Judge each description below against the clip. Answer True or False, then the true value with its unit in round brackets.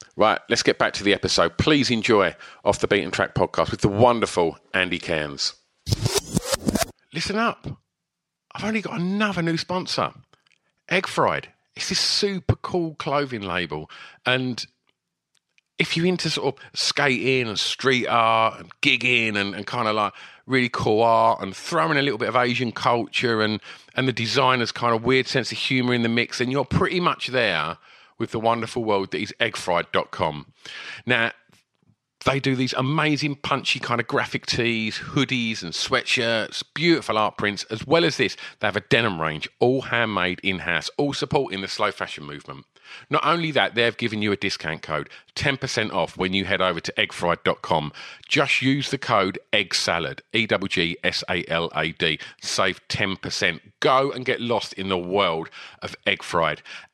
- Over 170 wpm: False (165 wpm)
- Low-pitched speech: True (120 Hz)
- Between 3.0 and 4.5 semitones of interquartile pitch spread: False (5.4 semitones)